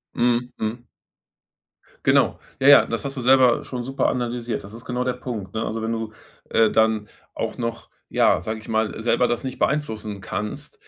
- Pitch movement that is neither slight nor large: No, narrow, 2.2 semitones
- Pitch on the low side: Yes, low, 115 Hz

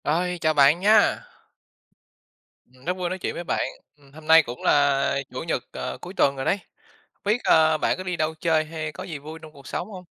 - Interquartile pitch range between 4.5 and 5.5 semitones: No, average, 3.8 semitones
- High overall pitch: No, medium, 155 Hz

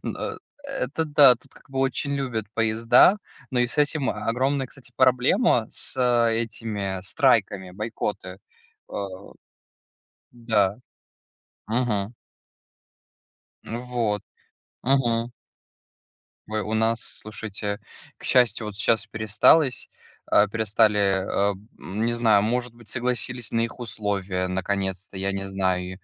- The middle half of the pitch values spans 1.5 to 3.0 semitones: No, average, 3.4 semitones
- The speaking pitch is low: Yes, low, 115 Hz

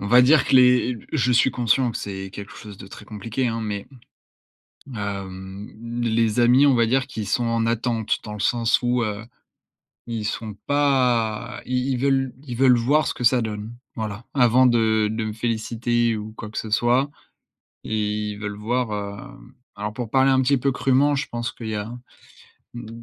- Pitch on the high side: No, low, 115 Hz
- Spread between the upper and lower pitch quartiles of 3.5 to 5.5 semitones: No, average, 2.8 semitones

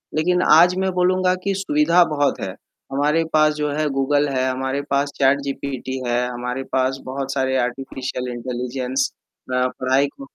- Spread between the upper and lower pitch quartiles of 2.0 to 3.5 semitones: Yes, average, 2.7 semitones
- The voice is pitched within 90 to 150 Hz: Yes, low, 135 Hz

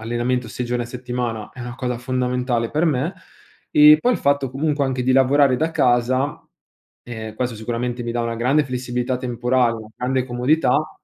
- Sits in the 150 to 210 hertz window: No, low, 125 Hz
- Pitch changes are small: Yes, narrow, 1.8 semitones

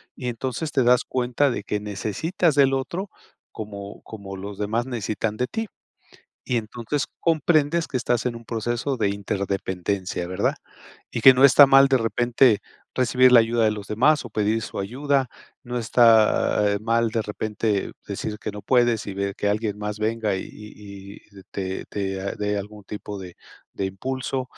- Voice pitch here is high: No, low, 110 Hz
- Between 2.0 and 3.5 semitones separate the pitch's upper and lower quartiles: No, average, 3.9 semitones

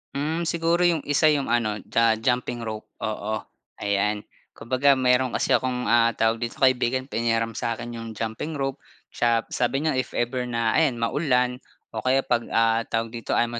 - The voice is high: No, low, 120 Hz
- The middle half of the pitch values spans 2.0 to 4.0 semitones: Yes, narrow, 2.6 semitones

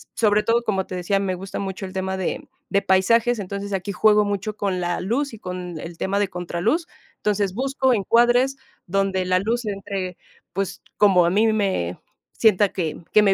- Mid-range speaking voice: No, high, 195 Hz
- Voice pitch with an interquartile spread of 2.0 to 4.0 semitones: Yes, narrow, 2.6 semitones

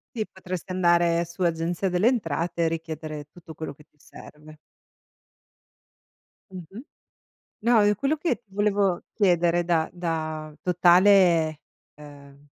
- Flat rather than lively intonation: No, average, 3.1 semitones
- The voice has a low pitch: No, medium, 175 Hz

